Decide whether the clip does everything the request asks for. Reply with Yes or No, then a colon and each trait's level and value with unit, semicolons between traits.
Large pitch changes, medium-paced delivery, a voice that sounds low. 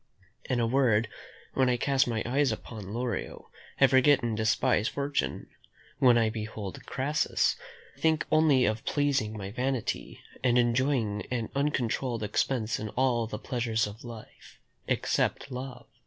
No: average, 3.4 semitones; average, 145 wpm; low, 120 Hz